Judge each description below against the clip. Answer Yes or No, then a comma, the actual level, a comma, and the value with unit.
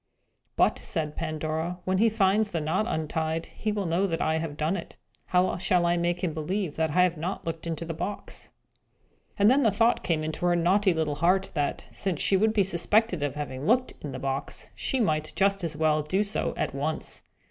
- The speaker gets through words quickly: Yes, fast, 215 wpm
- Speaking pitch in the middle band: Yes, medium, 170 Hz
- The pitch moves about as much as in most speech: Yes, average, 3.8 semitones